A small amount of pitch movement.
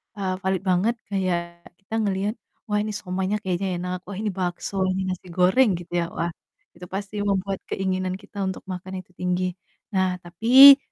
Yes: narrow, 1.8 semitones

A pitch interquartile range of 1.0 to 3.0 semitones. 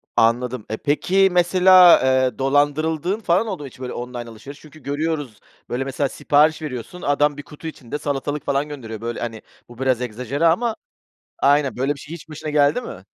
No: average, 3.8 semitones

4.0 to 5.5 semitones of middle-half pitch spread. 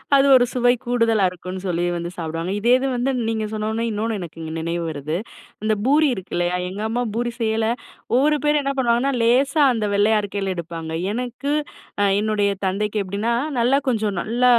Yes: average, 4.7 semitones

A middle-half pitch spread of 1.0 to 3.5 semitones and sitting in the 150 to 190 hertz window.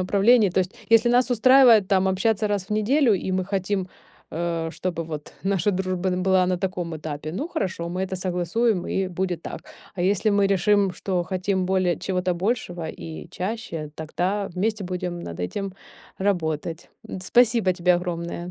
Yes: narrow, 2.5 semitones; medium, 185 Hz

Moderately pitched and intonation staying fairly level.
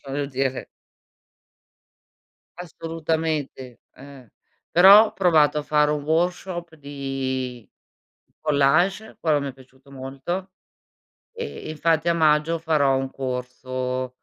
No: medium, 150 Hz; average, 3.7 semitones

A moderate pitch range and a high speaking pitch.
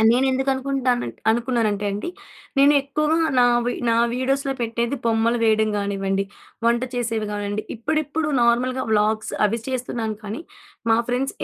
Yes: average, 3.4 semitones; high, 235 Hz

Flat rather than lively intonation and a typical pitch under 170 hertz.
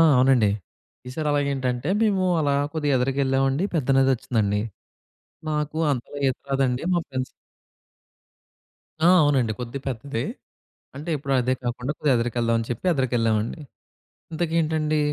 No: average, 3.2 semitones; low, 135 Hz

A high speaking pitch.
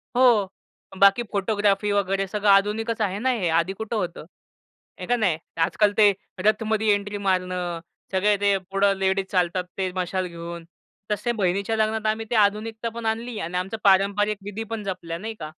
Yes: high, 200 Hz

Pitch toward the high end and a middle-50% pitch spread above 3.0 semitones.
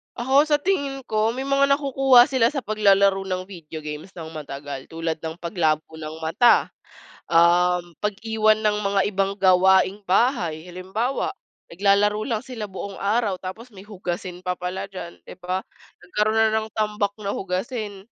Yes: high, 195 Hz; average, 3.7 semitones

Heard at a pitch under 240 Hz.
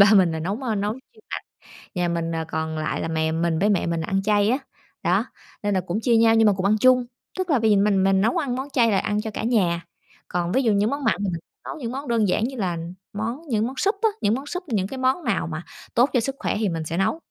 Yes: high, 210 Hz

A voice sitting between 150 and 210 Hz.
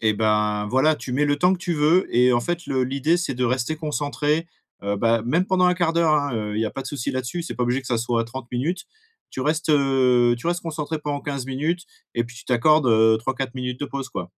No: low, 135 Hz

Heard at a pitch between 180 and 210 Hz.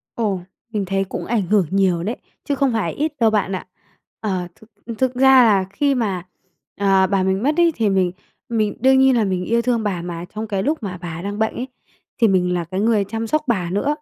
Yes: high, 205 Hz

